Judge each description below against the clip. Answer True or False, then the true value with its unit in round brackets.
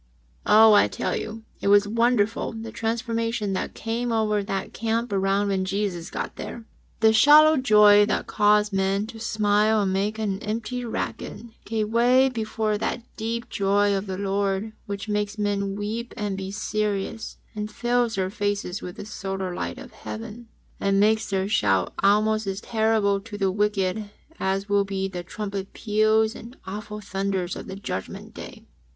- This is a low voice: False (210 Hz)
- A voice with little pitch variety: True (2.0 semitones)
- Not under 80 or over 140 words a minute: False (170 wpm)